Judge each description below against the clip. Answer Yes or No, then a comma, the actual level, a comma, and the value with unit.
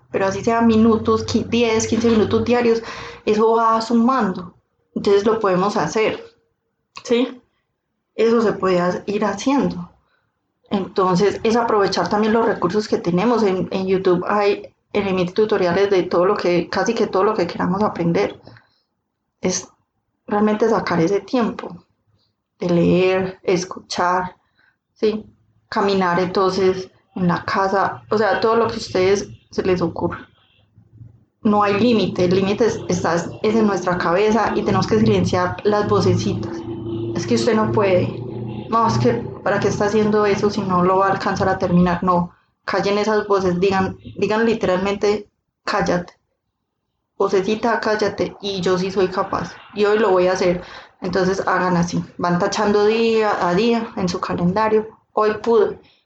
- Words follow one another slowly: No, average, 150 wpm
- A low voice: No, high, 200 Hz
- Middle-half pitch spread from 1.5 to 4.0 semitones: Yes, average, 3.2 semitones